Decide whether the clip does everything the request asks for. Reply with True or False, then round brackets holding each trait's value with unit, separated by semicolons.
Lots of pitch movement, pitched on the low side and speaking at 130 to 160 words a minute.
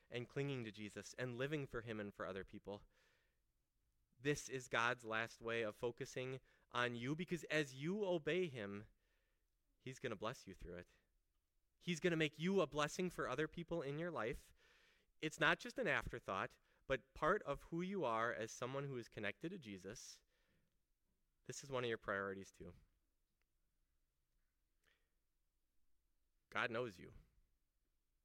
True (7.5 semitones; 120 Hz; 155 wpm)